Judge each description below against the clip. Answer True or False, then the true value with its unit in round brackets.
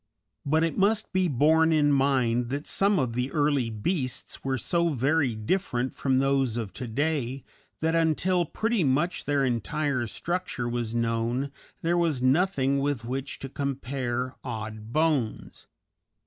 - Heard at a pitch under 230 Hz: True (135 Hz)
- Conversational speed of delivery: True (150 wpm)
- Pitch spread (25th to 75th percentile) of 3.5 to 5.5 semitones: True (4.7 semitones)